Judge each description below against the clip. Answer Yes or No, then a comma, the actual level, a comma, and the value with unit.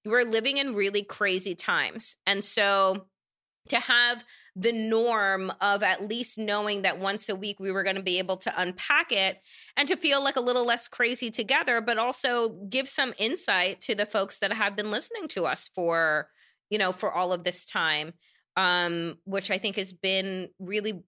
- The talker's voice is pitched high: Yes, high, 205 Hz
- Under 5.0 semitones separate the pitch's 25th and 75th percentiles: Yes, average, 3.7 semitones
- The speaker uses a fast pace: No, average, 190 wpm